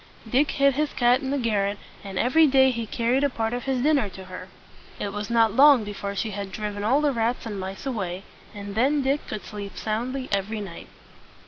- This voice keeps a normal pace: No, fast, 215 wpm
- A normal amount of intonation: Yes, average, 4.7 semitones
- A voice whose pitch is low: No, high, 225 Hz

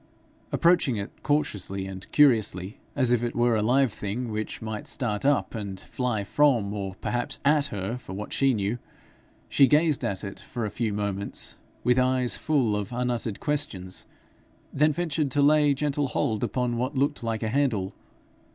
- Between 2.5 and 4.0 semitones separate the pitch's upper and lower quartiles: No, average, 5.3 semitones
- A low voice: Yes, low, 120 Hz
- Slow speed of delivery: No, average, 170 wpm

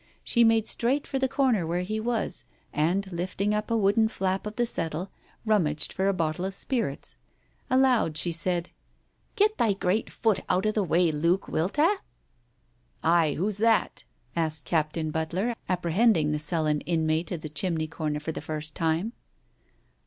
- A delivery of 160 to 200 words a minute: Yes, average, 175 wpm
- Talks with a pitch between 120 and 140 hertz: No, medium, 180 Hz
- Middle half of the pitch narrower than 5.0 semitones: No, average, 5.3 semitones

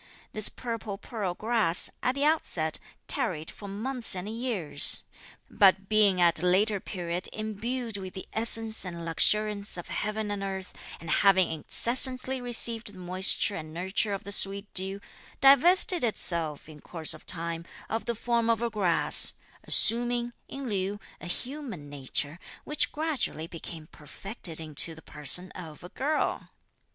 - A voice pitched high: Yes, high, 200 Hz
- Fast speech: No, average, 150 wpm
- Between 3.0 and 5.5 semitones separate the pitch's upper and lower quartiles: Yes, average, 5.0 semitones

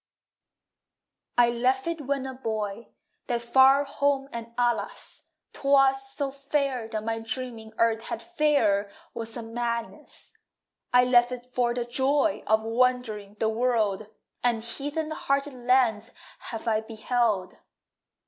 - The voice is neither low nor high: No, high, 245 Hz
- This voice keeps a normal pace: No, slow, 130 wpm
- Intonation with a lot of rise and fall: No, average, 3.1 semitones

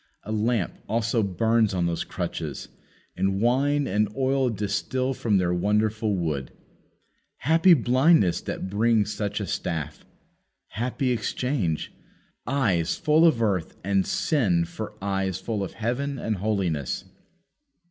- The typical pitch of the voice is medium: No, low, 110 Hz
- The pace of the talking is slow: Yes, slow, 125 wpm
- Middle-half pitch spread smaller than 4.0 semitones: No, average, 4.8 semitones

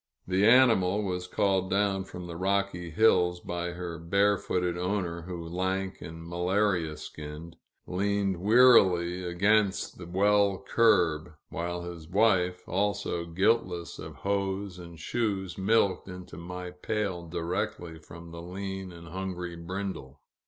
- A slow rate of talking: Yes, slow, 130 wpm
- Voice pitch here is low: Yes, very low, 90 Hz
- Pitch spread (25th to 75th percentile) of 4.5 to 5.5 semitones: No, narrow, 2.4 semitones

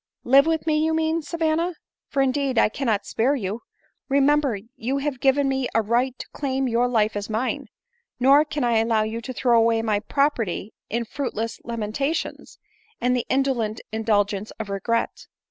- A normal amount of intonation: Yes, average, 3.9 semitones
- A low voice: No, high, 245 Hz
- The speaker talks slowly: No, average, 175 wpm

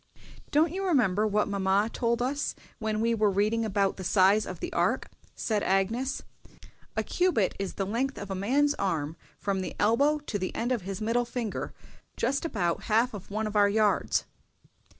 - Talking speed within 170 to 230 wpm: Yes, average, 185 wpm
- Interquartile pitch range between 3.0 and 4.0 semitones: Yes, average, 3.6 semitones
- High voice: Yes, high, 215 Hz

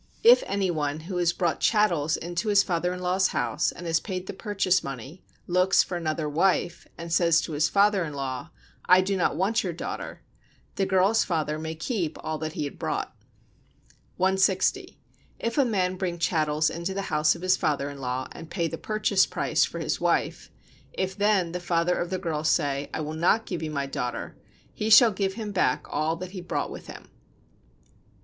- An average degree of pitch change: Yes, average, 3.4 semitones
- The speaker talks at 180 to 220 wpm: Yes, average, 200 wpm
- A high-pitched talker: No, medium, 175 Hz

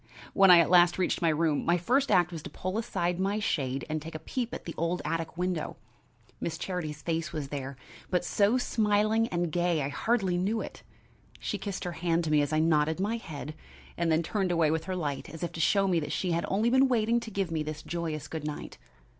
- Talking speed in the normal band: No, fast, 230 wpm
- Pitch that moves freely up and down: No, average, 3.7 semitones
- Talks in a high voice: No, medium, 170 Hz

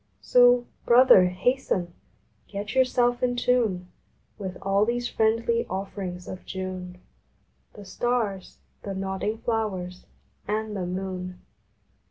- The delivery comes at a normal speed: No, slow, 110 wpm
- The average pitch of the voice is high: Yes, high, 200 Hz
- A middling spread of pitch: Yes, average, 4.5 semitones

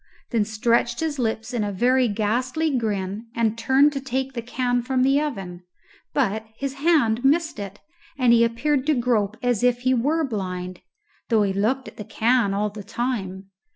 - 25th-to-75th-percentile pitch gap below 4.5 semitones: Yes, average, 3.9 semitones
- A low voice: No, high, 235 Hz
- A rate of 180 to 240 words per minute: Yes, average, 185 wpm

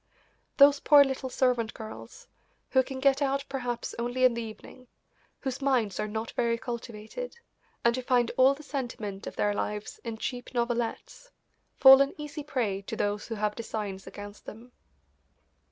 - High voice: Yes, high, 245 Hz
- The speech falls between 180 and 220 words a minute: No, average, 165 wpm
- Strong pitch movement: No, average, 3.5 semitones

